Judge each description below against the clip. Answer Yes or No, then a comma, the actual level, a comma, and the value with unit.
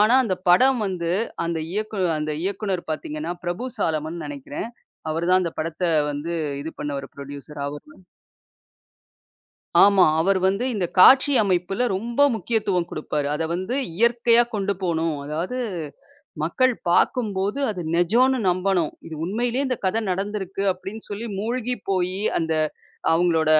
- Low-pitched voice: No, medium, 185 Hz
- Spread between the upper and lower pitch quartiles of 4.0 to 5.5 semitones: Yes, average, 4.9 semitones